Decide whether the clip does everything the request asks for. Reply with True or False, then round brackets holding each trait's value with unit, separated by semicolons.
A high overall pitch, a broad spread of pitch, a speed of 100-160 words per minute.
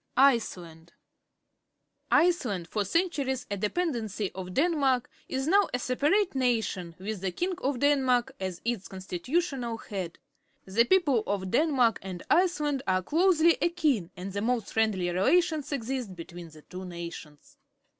True (235 Hz; 7.6 semitones; 140 wpm)